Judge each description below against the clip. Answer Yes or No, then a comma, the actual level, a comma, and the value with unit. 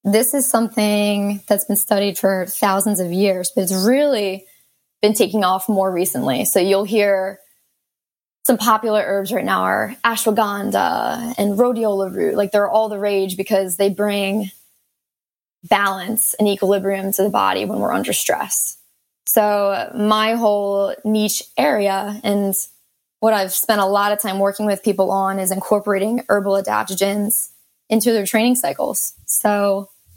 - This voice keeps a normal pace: Yes, average, 150 wpm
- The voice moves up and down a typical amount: No, narrow, 1.6 semitones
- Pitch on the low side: No, high, 205 Hz